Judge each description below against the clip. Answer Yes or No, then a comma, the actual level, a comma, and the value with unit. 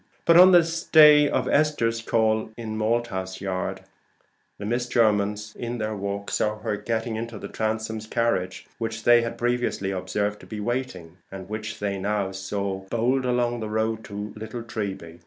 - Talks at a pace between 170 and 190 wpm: Yes, average, 175 wpm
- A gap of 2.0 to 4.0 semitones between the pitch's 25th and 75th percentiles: Yes, average, 2.7 semitones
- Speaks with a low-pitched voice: Yes, low, 110 Hz